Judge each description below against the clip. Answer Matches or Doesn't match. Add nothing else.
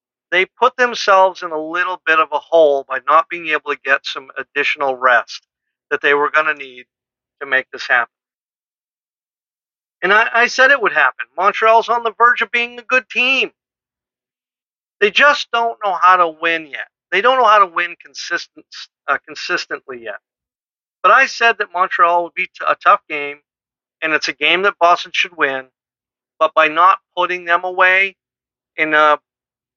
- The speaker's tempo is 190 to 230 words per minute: Doesn't match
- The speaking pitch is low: Doesn't match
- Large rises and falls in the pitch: Matches